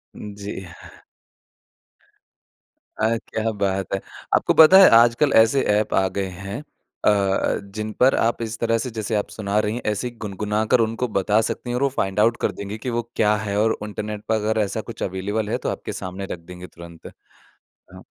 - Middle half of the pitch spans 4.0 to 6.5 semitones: No, narrow, 2.4 semitones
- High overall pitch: No, low, 105 Hz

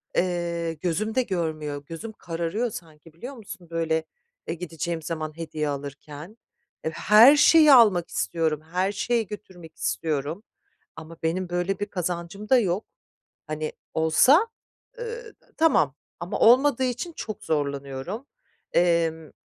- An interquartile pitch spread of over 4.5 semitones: Yes, average, 5.1 semitones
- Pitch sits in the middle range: Yes, medium, 170 Hz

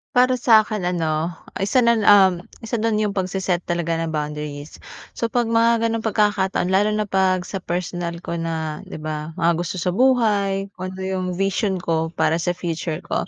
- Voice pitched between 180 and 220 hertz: Yes, medium, 185 Hz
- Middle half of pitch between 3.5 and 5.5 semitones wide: Yes, average, 4.0 semitones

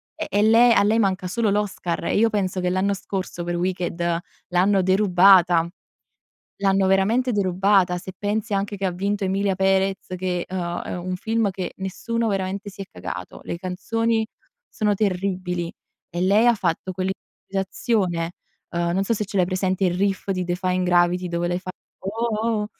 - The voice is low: No, high, 190 Hz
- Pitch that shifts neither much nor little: No, narrow, 2.2 semitones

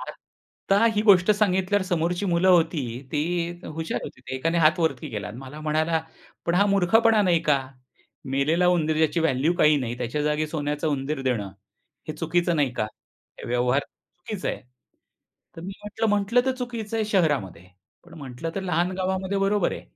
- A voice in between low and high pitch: Yes, medium, 170 Hz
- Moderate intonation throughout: Yes, average, 4.3 semitones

